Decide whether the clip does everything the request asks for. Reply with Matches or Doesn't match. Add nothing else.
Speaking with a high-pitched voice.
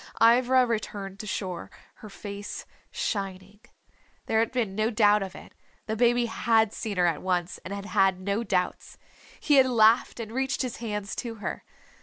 Matches